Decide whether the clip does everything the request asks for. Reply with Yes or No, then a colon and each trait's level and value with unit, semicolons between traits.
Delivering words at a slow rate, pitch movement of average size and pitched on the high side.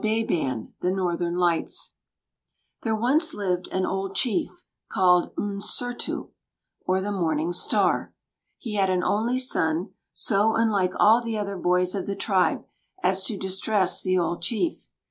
No: average, 145 wpm; average, 3.5 semitones; high, 195 Hz